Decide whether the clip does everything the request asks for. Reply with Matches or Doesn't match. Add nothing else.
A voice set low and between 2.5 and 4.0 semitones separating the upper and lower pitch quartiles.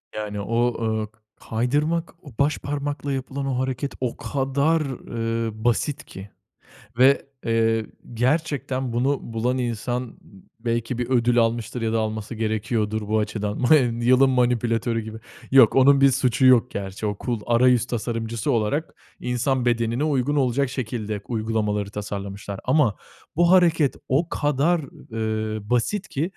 Matches